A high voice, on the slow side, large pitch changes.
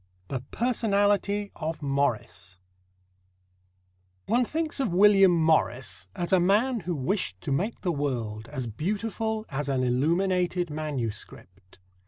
No: medium, 170 Hz; slow, 120 wpm; wide, 7.3 semitones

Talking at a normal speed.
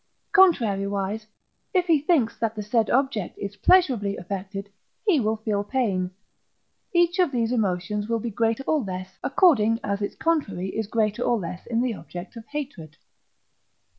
Yes: average, 160 wpm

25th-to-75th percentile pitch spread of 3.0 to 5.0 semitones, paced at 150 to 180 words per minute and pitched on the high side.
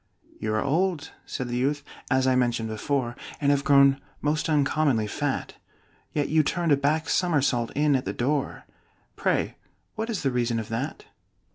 No: average, 3.5 semitones; average, 170 wpm; medium, 140 Hz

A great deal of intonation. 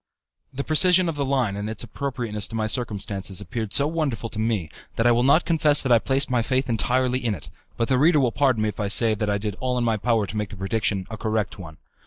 No: average, 3.9 semitones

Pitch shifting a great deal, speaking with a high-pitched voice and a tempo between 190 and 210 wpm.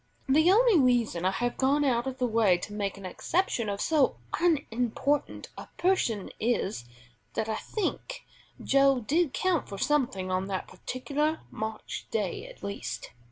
No: wide, 6.4 semitones; very high, 255 Hz; average, 160 wpm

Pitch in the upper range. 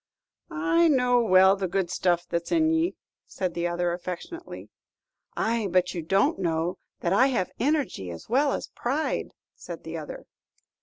Yes: high, 195 Hz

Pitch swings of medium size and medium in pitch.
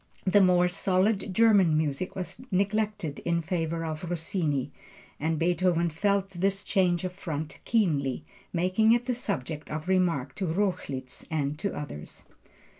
Yes: average, 3.7 semitones; medium, 180 Hz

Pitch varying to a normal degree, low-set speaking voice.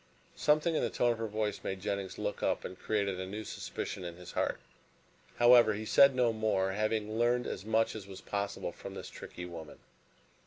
Yes: average, 3.0 semitones; low, 110 Hz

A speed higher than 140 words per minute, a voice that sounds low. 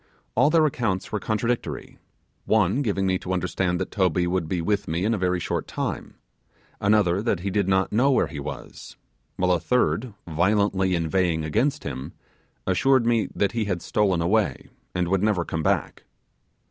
Yes: average, 175 wpm; very low, 95 Hz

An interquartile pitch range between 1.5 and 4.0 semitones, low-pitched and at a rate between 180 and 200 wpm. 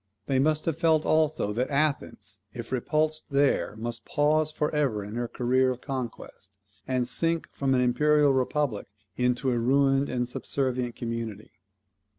No: average, 3.6 semitones; low, 130 Hz; average, 155 wpm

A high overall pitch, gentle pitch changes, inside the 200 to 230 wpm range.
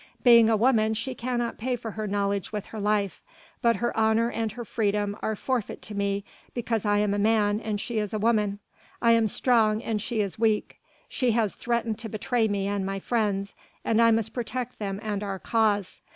Yes: high, 220 Hz; narrow, 2.1 semitones; fast, 205 wpm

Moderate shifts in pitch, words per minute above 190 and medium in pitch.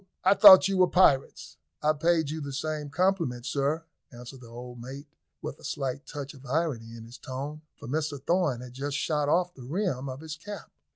Yes: average, 4.0 semitones; fast, 205 wpm; medium, 145 Hz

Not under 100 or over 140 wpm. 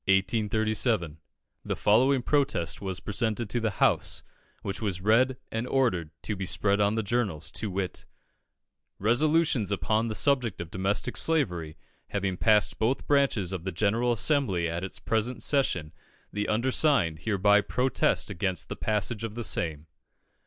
No: average, 150 wpm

